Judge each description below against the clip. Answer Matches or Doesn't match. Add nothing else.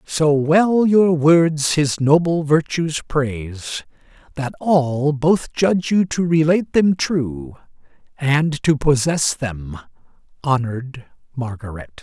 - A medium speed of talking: Doesn't match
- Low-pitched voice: Doesn't match